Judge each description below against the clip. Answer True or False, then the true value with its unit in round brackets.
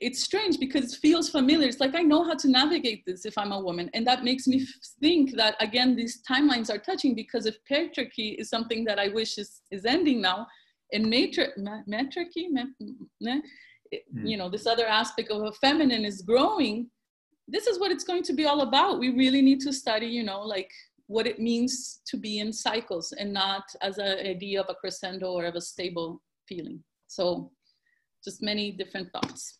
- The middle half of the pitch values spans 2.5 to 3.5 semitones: False (5.0 semitones)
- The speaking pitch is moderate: False (235 Hz)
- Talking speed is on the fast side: True (195 wpm)